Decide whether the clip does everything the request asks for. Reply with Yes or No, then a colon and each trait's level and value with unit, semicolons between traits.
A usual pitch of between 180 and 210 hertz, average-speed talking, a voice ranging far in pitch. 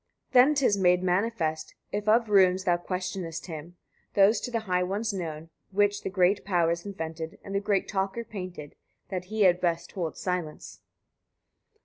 No: medium, 185 Hz; average, 165 wpm; average, 2.9 semitones